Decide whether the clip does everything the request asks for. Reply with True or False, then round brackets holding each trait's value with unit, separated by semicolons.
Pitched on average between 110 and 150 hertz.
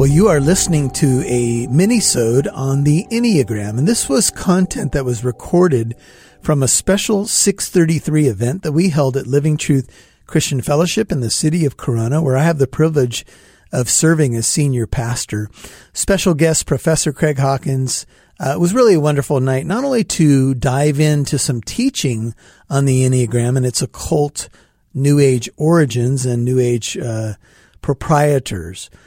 True (140 Hz)